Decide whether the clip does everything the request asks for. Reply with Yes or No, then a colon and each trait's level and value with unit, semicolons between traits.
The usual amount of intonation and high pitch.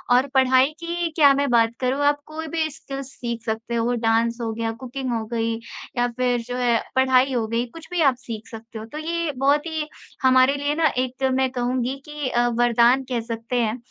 Yes: average, 3.2 semitones; very high, 255 Hz